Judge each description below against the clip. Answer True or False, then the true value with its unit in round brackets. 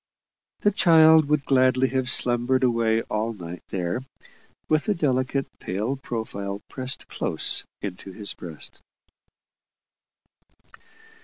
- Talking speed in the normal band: False (105 wpm)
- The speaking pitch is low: True (125 Hz)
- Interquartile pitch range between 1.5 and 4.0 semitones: False (4.9 semitones)